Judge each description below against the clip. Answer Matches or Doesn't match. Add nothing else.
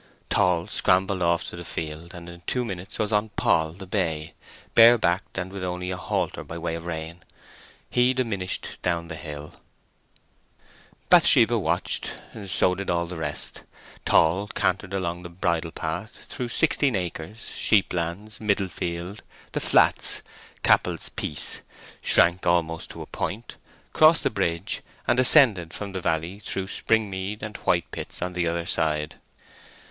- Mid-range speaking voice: Doesn't match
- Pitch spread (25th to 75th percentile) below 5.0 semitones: Matches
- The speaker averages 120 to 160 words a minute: Matches